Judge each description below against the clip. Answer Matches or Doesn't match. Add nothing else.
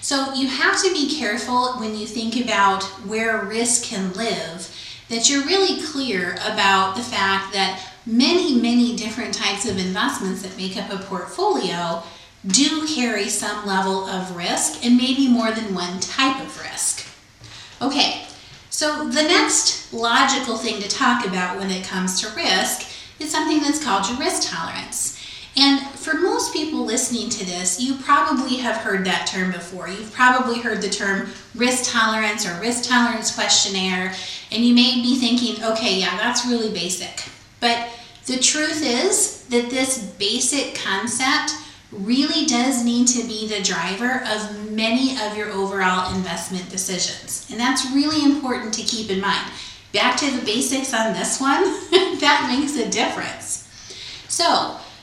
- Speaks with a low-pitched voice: Doesn't match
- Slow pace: Doesn't match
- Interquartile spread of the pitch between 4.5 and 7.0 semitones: Matches